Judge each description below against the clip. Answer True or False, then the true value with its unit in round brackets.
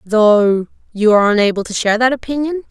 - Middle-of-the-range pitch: False (225 Hz)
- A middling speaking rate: True (175 wpm)